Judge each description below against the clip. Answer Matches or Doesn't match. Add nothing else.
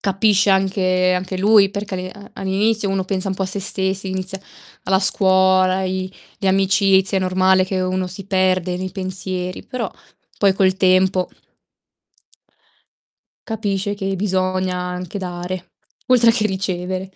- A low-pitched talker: Doesn't match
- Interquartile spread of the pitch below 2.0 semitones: Matches